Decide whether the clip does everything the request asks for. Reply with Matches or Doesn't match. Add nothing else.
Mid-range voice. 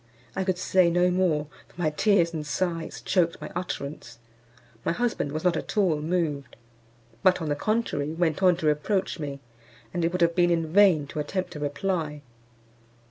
Matches